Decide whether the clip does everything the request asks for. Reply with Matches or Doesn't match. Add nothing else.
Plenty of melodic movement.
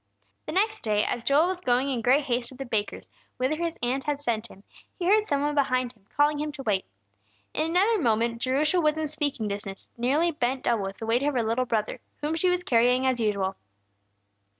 Doesn't match